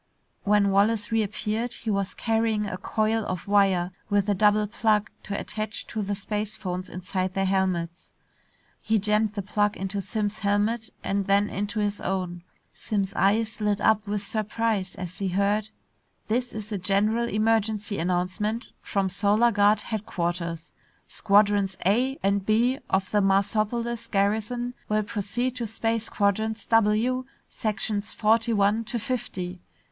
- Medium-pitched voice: No, high, 210 Hz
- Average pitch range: No, narrow, 1.9 semitones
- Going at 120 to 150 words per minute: Yes, average, 145 wpm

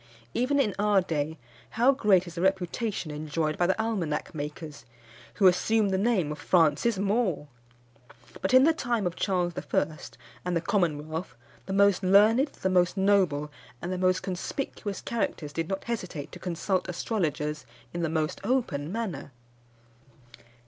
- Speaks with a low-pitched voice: No, medium, 185 Hz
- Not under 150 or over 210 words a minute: Yes, average, 155 wpm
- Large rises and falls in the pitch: No, average, 4.7 semitones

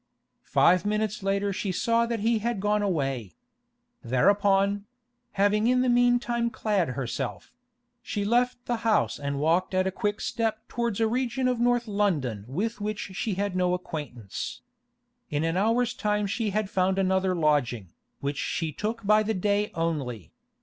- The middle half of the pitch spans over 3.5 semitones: Yes, average, 4.4 semitones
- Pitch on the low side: No, high, 205 Hz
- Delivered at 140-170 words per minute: Yes, average, 155 wpm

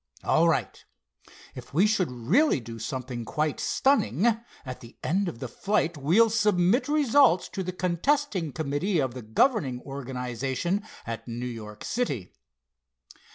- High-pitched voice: No, medium, 155 Hz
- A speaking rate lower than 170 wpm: Yes, average, 140 wpm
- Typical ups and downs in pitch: No, wide, 8.9 semitones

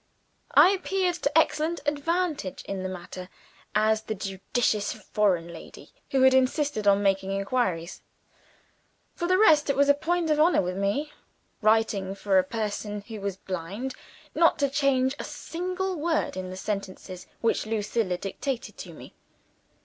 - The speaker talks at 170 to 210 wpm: No, average, 155 wpm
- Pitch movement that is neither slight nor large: No, wide, 7.4 semitones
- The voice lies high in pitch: Yes, high, 220 Hz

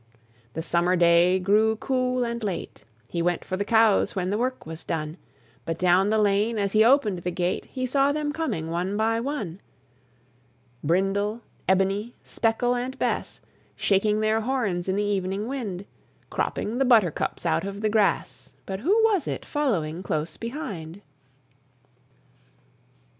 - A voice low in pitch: No, high, 205 Hz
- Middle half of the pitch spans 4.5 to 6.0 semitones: Yes, average, 4.8 semitones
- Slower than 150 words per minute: No, average, 155 wpm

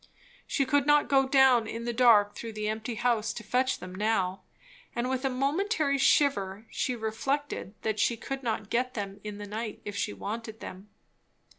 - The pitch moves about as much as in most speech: Yes, average, 3.9 semitones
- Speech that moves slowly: No, average, 185 wpm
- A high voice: Yes, high, 230 Hz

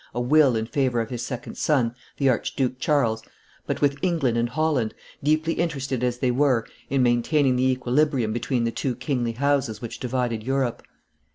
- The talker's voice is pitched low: Yes, low, 130 Hz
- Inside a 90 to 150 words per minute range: No, average, 175 wpm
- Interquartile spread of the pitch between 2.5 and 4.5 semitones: Yes, average, 2.9 semitones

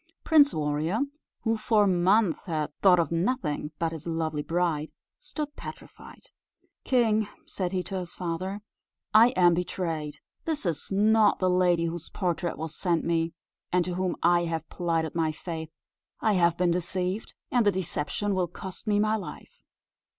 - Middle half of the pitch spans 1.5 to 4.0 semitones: Yes, average, 3.7 semitones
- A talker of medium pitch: Yes, medium, 180 Hz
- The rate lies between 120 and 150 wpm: No, average, 160 wpm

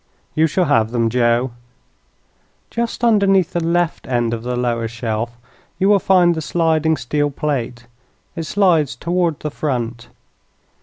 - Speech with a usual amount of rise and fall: No, wide, 6.4 semitones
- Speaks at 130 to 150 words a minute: Yes, average, 145 wpm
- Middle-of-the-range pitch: Yes, medium, 150 Hz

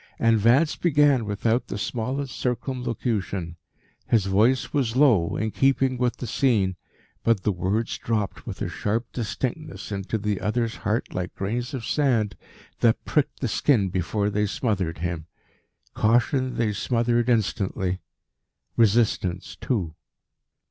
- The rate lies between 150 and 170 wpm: No, slow, 135 wpm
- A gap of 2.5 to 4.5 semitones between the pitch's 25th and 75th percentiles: Yes, average, 3.8 semitones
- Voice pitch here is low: Yes, low, 115 Hz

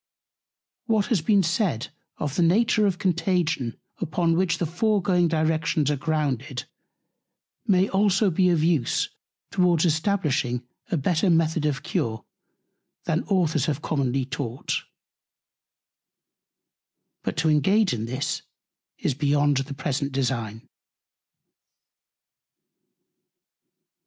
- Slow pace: Yes, slow, 105 wpm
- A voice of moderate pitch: Yes, medium, 160 Hz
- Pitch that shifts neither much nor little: Yes, average, 4.7 semitones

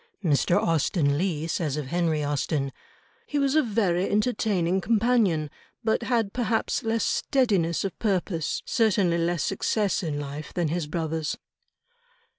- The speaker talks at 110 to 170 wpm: Yes, slow, 135 wpm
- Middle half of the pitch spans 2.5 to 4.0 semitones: No, wide, 5.6 semitones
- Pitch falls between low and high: Yes, medium, 175 Hz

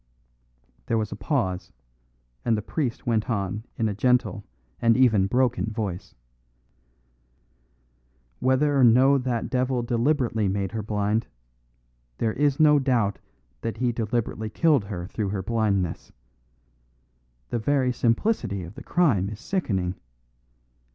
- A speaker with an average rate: No, slow, 130 wpm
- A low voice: Yes, low, 115 Hz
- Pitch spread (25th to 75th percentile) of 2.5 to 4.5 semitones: Yes, average, 3.8 semitones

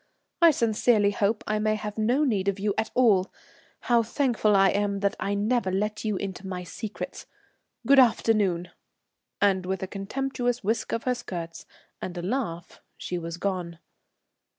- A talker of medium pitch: No, high, 205 Hz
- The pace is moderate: Yes, average, 165 wpm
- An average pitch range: Yes, average, 3.3 semitones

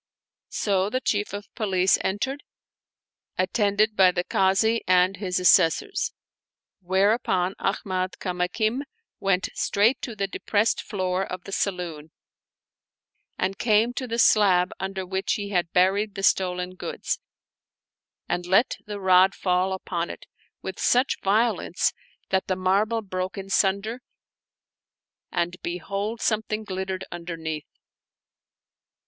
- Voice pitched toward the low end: No, high, 190 Hz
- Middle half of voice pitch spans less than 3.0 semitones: Yes, narrow, 2.5 semitones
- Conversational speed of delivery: No, slow, 120 wpm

